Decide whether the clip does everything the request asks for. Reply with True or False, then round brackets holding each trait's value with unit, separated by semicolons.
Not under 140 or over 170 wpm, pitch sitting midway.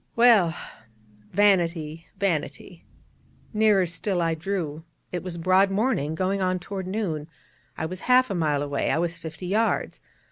True (150 wpm; 180 Hz)